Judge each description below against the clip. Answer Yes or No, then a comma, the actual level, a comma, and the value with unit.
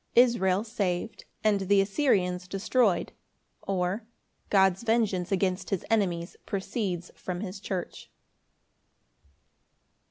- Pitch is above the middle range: Yes, high, 195 Hz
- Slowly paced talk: Yes, slow, 95 wpm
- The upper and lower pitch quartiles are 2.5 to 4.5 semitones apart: Yes, average, 2.9 semitones